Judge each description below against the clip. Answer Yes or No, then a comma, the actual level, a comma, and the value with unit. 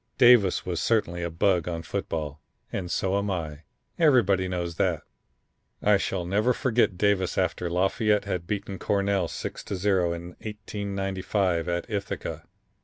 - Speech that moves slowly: No, average, 145 wpm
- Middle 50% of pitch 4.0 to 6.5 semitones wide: No, average, 2.8 semitones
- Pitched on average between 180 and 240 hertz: No, very low, 95 Hz